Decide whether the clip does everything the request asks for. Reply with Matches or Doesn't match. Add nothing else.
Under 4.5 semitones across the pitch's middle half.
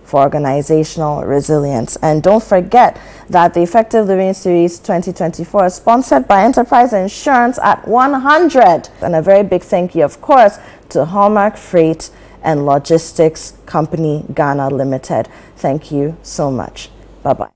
Doesn't match